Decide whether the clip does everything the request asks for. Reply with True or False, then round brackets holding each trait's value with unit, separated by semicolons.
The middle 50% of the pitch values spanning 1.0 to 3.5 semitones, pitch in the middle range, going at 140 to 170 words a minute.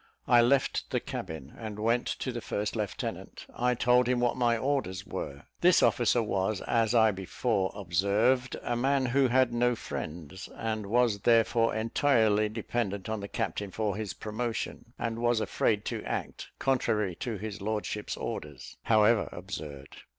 False (3.1 semitones; 110 Hz; 160 wpm)